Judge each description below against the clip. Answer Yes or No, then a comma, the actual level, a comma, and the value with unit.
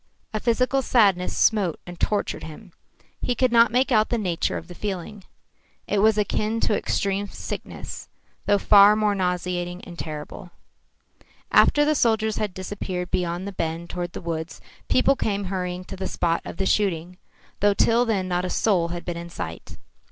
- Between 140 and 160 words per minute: No, average, 175 wpm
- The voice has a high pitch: Yes, high, 195 Hz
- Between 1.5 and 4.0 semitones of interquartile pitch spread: Yes, average, 3.4 semitones